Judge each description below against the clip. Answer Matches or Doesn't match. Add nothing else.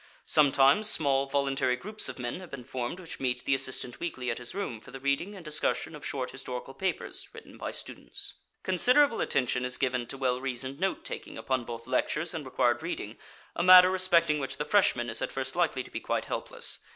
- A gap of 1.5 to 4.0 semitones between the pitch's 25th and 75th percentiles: Doesn't match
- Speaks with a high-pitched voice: Doesn't match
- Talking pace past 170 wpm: Matches